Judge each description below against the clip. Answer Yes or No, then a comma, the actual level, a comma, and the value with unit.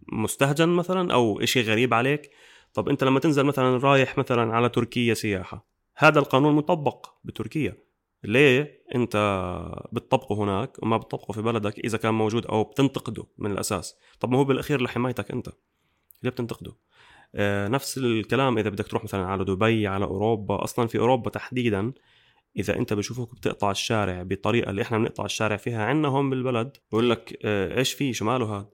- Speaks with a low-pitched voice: Yes, low, 115 Hz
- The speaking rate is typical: No, fast, 165 wpm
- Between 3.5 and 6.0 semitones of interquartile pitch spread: Yes, average, 3.8 semitones